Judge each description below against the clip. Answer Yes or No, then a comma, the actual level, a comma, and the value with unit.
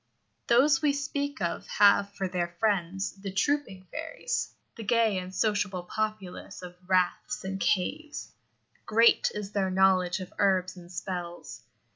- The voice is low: No, high, 195 Hz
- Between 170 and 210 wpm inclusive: No, average, 140 wpm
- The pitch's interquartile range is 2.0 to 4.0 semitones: Yes, average, 3.4 semitones